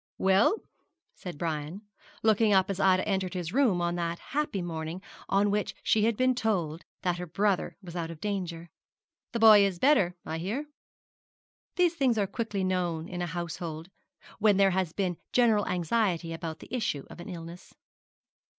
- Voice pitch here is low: No, medium, 185 Hz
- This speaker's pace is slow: No, average, 170 wpm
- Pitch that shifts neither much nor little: Yes, average, 3.6 semitones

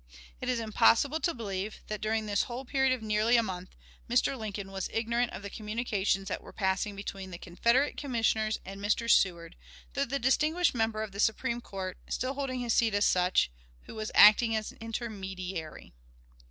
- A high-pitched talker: Yes, high, 220 Hz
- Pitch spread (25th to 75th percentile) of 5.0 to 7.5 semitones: No, average, 3.5 semitones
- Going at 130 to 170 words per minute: No, average, 180 wpm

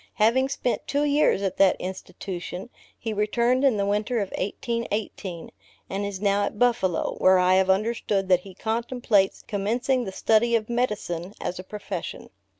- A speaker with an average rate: Yes, average, 160 wpm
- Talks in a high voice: Yes, high, 210 Hz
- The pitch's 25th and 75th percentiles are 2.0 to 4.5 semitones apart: Yes, average, 3.7 semitones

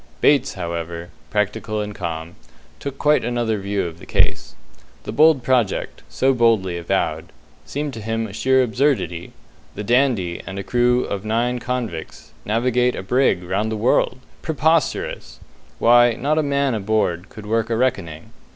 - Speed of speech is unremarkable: Yes, average, 155 wpm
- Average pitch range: Yes, average, 4.6 semitones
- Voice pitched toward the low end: Yes, low, 115 Hz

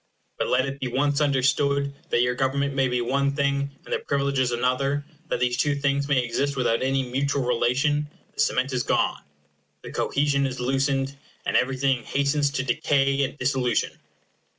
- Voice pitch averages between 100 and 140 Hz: Yes, low, 135 Hz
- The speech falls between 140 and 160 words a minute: No, average, 175 wpm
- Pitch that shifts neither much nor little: No, narrow, 1.7 semitones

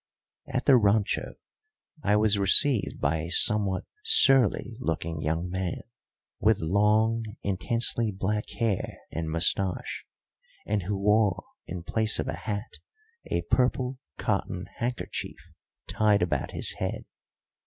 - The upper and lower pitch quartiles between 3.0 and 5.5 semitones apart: Yes, average, 3.7 semitones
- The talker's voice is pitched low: Yes, low, 105 Hz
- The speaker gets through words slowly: Yes, slow, 120 wpm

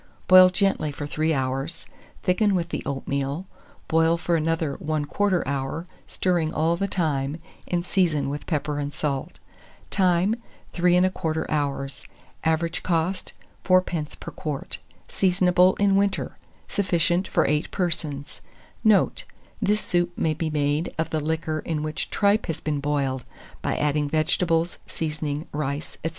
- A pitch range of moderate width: Yes, average, 3.3 semitones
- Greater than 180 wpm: No, average, 140 wpm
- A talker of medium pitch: Yes, medium, 160 Hz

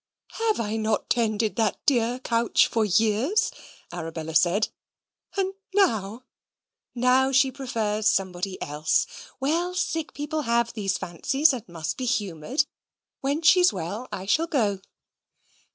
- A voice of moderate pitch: No, high, 230 Hz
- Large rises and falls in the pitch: Yes, wide, 5.7 semitones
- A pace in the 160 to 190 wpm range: No, slow, 135 wpm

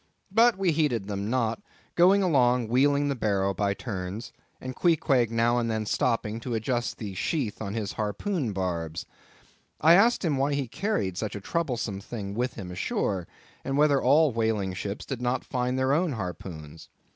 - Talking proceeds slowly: No, average, 175 wpm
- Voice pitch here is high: No, low, 120 Hz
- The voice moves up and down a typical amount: No, wide, 5.9 semitones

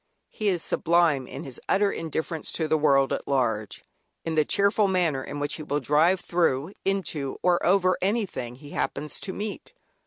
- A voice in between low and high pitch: Yes, medium, 160 Hz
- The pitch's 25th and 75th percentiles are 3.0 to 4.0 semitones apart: No, average, 4.6 semitones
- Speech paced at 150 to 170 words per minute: No, average, 180 wpm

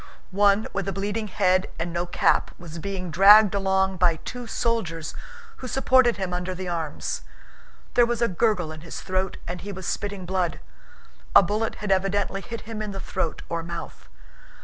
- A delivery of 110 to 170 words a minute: No, average, 180 wpm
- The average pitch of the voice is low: No, high, 190 Hz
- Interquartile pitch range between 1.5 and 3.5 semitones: Yes, average, 2.8 semitones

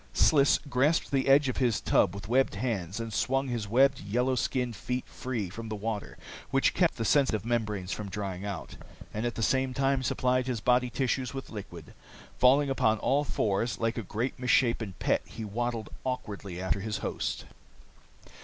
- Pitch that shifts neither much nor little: Yes, average, 3.7 semitones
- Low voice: Yes, low, 120 Hz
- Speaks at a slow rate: No, average, 175 wpm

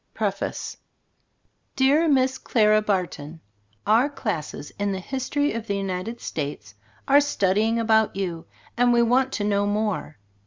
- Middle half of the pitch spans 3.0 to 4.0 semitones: No, average, 4.7 semitones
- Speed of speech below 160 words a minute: Yes, average, 140 wpm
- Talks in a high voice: Yes, high, 215 Hz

